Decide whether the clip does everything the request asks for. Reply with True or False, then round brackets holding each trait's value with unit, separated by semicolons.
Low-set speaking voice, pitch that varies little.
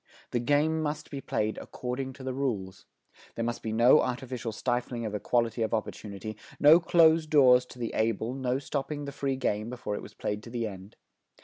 False (125 Hz; 3.7 semitones)